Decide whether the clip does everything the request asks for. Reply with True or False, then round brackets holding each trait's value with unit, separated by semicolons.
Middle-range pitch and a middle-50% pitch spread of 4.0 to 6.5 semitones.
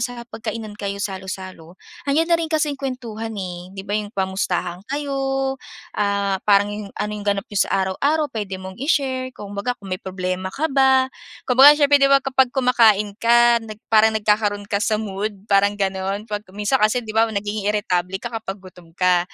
False (210 Hz; 4.3 semitones)